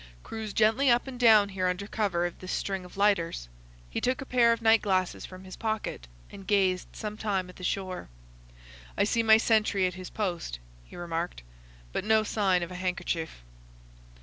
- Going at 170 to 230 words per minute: Yes, average, 190 wpm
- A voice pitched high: Yes, high, 195 Hz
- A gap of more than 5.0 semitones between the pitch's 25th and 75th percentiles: No, average, 3.2 semitones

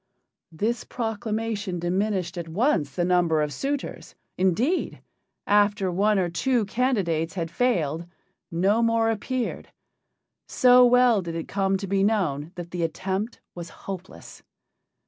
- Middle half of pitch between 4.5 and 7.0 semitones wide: Yes, average, 4.8 semitones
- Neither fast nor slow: No, slow, 130 wpm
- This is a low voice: No, high, 195 Hz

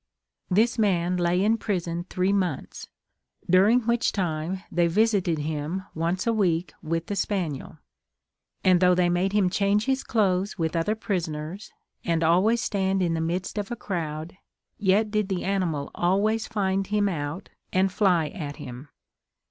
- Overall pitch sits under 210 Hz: Yes, medium, 185 Hz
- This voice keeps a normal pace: Yes, average, 155 wpm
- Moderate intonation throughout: Yes, average, 3.4 semitones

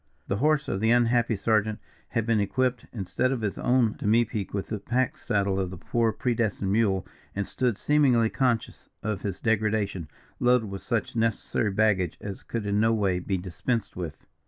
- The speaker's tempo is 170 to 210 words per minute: Yes, average, 180 wpm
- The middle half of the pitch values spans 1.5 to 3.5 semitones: Yes, average, 3.2 semitones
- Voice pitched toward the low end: Yes, low, 110 Hz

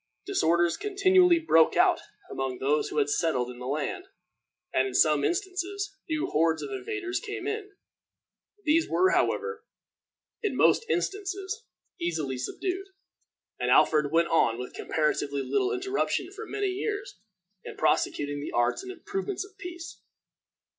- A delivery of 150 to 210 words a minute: No, average, 140 wpm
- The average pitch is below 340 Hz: No, very high, 355 Hz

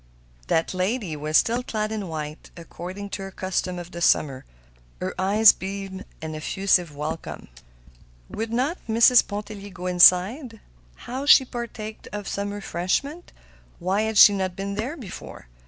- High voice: Yes, high, 195 Hz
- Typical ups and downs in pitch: Yes, average, 3.6 semitones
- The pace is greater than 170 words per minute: No, average, 150 wpm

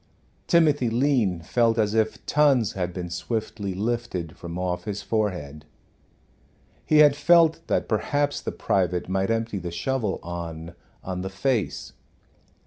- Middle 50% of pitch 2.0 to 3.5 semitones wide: No, wide, 5.6 semitones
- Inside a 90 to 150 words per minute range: Yes, slow, 135 wpm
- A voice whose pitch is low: Yes, low, 105 Hz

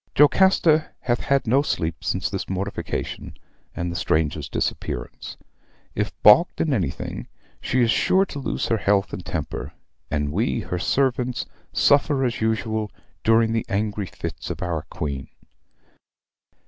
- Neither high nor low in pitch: No, low, 110 Hz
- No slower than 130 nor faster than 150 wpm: Yes, average, 140 wpm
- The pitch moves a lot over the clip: Yes, wide, 7.1 semitones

